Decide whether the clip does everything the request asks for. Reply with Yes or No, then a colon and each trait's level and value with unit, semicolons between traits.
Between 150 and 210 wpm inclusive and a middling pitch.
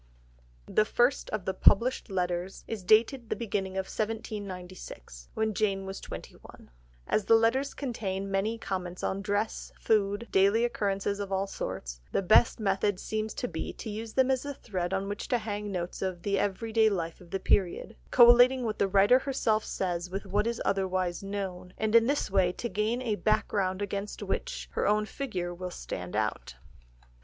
No: average, 180 wpm; high, 200 Hz